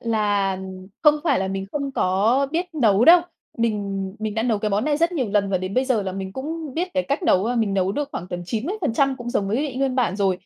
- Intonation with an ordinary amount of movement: No, wide, 6.0 semitones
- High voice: Yes, high, 225 Hz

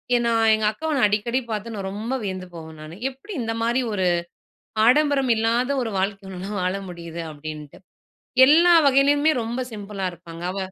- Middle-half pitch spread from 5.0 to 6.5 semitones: Yes, wide, 5.6 semitones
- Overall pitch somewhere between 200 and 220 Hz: Yes, high, 215 Hz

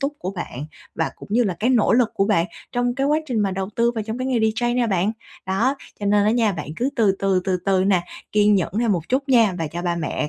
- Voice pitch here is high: Yes, high, 210 Hz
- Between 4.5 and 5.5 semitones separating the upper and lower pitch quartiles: No, average, 4.1 semitones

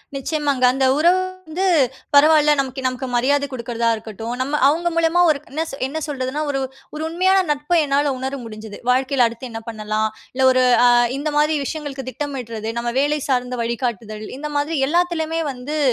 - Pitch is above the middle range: Yes, very high, 275 Hz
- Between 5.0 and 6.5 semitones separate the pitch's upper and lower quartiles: No, average, 3.8 semitones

